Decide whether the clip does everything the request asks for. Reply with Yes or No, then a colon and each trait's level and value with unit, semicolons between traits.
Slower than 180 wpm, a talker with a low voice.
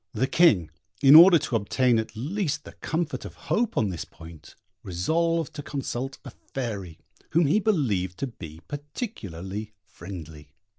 Yes: average, 150 wpm; low, 125 Hz